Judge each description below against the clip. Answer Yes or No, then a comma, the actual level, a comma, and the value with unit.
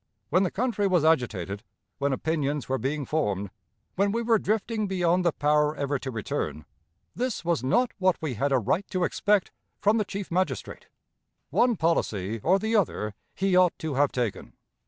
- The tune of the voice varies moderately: No, wide, 6.6 semitones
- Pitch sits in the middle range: Yes, medium, 165 Hz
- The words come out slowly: No, average, 175 wpm